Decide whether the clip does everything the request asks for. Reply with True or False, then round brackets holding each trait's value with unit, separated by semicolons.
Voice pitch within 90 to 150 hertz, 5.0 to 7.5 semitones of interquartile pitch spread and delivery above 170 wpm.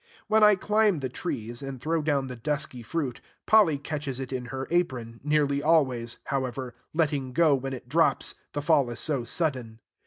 False (140 Hz; 3.8 semitones; 180 wpm)